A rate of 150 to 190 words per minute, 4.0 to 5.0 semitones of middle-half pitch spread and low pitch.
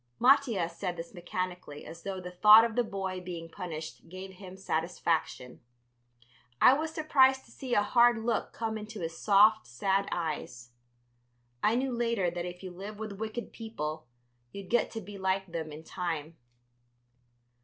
No: average, 165 wpm; average, 4.6 semitones; high, 190 Hz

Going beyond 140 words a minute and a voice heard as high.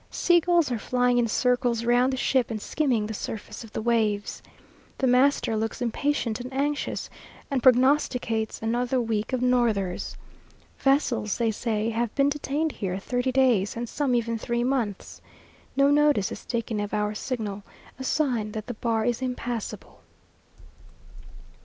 Yes: average, 155 wpm; high, 240 Hz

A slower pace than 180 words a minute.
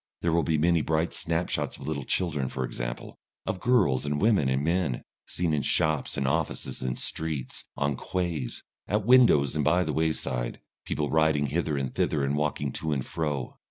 No: average, 185 wpm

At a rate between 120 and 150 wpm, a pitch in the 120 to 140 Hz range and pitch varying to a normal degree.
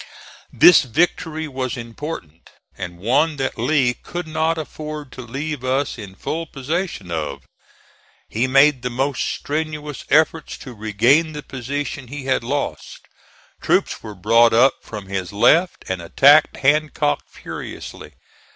Yes: slow, 135 wpm; low, 135 Hz; average, 4.9 semitones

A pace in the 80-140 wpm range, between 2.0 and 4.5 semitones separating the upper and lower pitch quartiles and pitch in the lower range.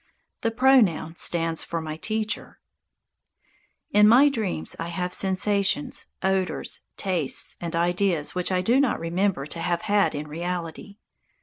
No: slow, 135 wpm; average, 4.0 semitones; medium, 185 Hz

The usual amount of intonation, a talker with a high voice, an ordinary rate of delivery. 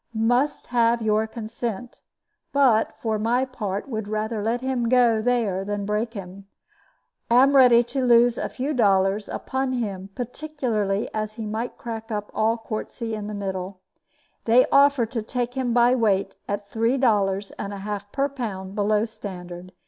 Yes: average, 3.2 semitones; high, 225 Hz; average, 165 wpm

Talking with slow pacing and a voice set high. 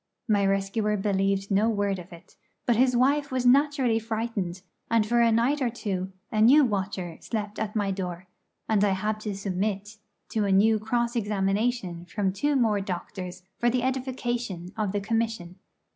No: average, 175 wpm; high, 210 Hz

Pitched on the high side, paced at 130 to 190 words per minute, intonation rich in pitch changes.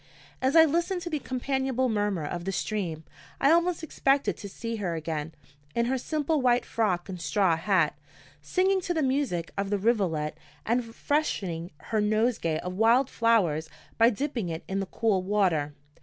Yes: high, 215 Hz; average, 170 wpm; wide, 7.0 semitones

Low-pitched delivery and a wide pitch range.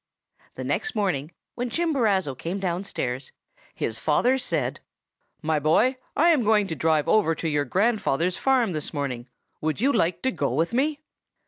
No: medium, 185 Hz; wide, 8.2 semitones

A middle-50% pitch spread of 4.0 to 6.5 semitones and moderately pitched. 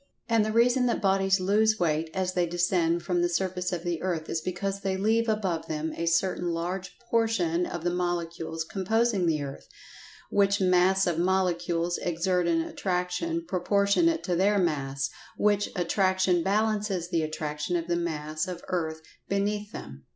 No: average, 2.9 semitones; medium, 180 Hz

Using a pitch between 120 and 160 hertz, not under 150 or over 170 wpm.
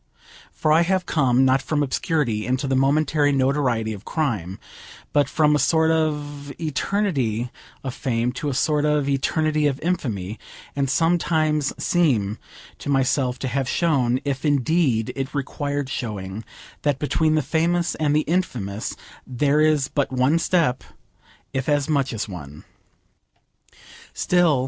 No: medium, 140 Hz; average, 140 wpm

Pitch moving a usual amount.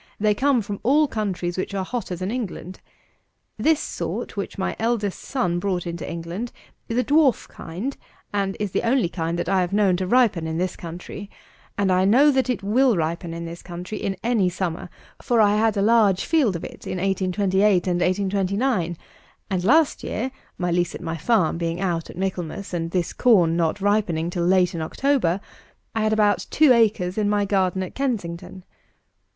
Yes: average, 4.1 semitones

